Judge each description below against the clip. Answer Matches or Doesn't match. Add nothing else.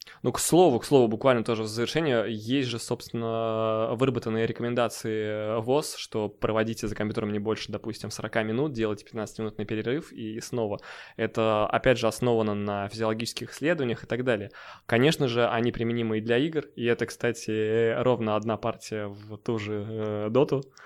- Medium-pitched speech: Doesn't match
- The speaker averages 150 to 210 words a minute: Matches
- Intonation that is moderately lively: Doesn't match